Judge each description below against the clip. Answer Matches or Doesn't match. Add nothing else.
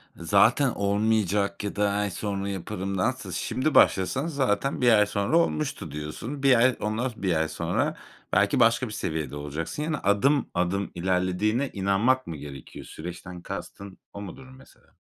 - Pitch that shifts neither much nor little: Doesn't match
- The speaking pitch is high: Doesn't match